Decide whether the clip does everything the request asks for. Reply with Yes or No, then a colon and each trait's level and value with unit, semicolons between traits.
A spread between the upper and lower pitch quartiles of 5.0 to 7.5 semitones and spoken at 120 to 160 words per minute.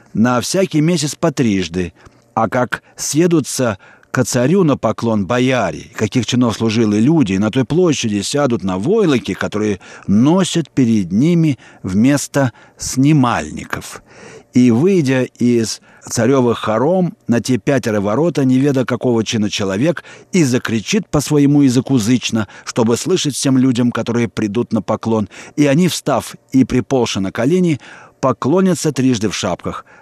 No: average, 4.6 semitones; average, 140 wpm